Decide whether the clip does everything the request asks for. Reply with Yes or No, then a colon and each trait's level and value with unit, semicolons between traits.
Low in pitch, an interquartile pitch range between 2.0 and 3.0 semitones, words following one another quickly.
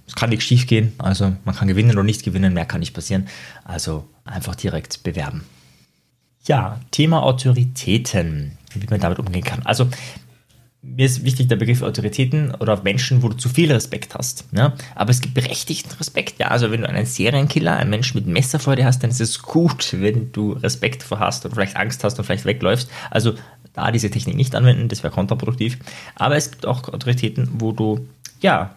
No: low, 120 Hz; average, 3.7 semitones; fast, 195 wpm